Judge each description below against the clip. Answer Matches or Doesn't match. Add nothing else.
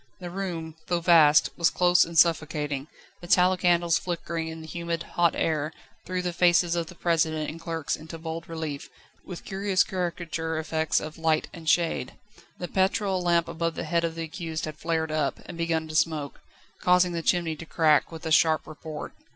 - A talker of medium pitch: Matches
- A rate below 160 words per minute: Doesn't match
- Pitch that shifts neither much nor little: Doesn't match